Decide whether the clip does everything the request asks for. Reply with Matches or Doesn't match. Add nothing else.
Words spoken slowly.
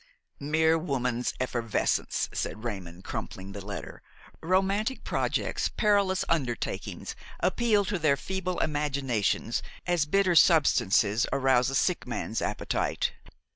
Matches